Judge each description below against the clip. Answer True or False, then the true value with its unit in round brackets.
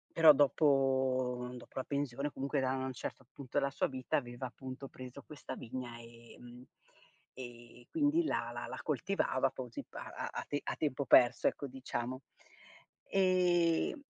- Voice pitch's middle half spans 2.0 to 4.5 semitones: True (2.6 semitones)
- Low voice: True (130 Hz)